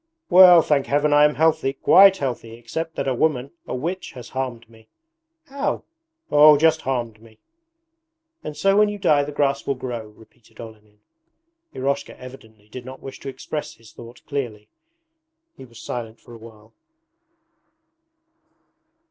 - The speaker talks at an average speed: Yes, average, 155 wpm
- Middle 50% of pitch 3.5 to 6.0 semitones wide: Yes, average, 4.6 semitones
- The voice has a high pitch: No, low, 130 Hz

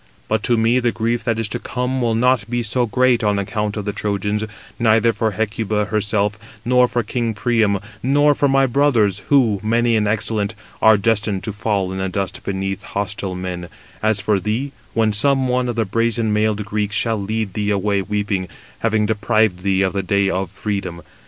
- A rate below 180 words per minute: No, average, 195 wpm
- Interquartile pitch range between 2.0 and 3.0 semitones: Yes, narrow, 2.6 semitones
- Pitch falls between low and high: No, low, 110 Hz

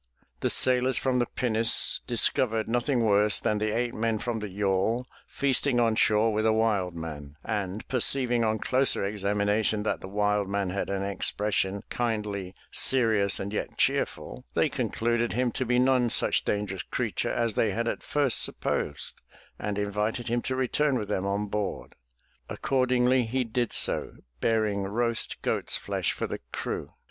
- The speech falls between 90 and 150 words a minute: No, average, 170 wpm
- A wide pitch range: No, average, 3.0 semitones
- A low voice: Yes, low, 110 Hz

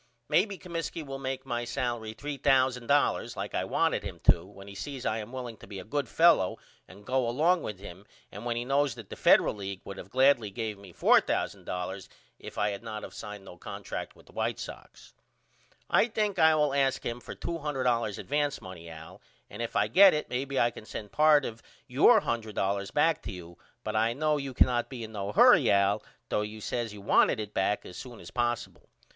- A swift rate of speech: Yes, fast, 210 wpm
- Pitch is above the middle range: No, low, 120 Hz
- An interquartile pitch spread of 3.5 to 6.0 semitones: Yes, average, 5.1 semitones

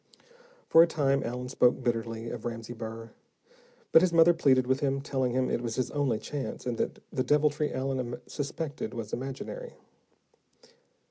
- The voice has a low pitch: Yes, low, 130 Hz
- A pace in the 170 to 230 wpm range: No, average, 160 wpm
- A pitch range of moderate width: Yes, average, 3.4 semitones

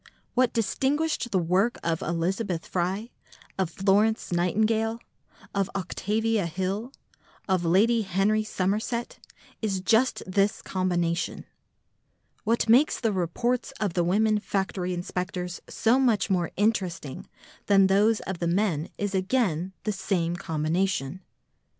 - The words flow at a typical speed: No, slow, 120 wpm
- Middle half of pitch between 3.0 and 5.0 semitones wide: Yes, average, 3.7 semitones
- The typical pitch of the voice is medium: No, high, 195 Hz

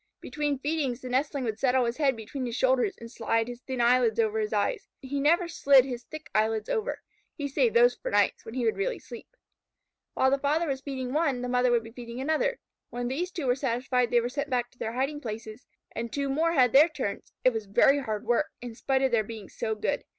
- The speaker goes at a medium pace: No, fast, 235 wpm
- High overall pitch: Yes, very high, 255 Hz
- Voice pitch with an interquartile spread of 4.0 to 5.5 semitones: No, average, 3.4 semitones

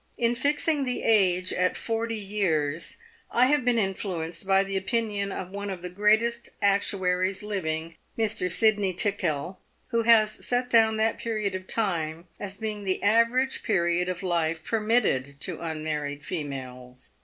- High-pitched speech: Yes, high, 195 Hz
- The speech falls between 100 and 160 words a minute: Yes, average, 150 wpm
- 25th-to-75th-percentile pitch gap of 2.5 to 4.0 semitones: No, average, 4.5 semitones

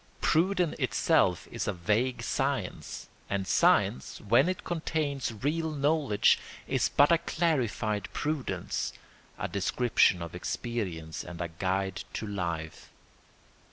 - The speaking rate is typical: No, slow, 120 wpm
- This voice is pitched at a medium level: No, low, 115 Hz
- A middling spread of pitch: No, wide, 8.5 semitones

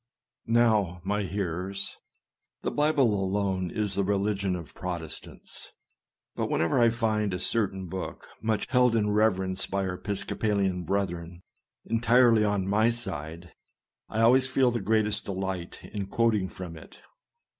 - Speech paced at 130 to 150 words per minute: Yes, average, 145 wpm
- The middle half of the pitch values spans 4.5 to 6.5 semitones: No, average, 3.2 semitones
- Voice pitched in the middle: No, low, 100 Hz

